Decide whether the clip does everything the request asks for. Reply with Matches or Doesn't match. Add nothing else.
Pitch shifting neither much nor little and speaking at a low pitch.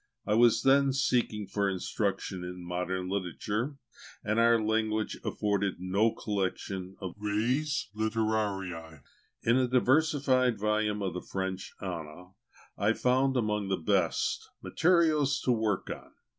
Matches